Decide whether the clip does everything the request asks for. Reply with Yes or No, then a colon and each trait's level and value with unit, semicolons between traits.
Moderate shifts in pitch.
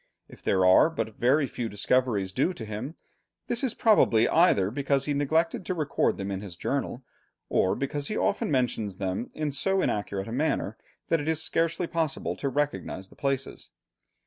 No: wide, 7.1 semitones